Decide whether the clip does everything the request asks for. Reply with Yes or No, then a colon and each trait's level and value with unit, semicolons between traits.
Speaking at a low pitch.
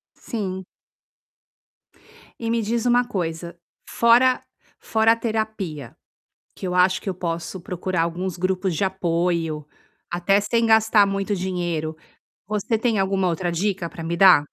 No: high, 190 Hz